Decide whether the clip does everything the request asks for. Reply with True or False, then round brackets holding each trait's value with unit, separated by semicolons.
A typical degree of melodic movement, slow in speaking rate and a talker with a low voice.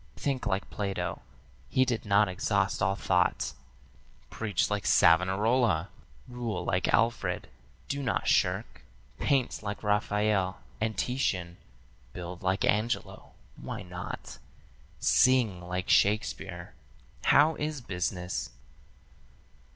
True (4.2 semitones; 105 wpm; 105 Hz)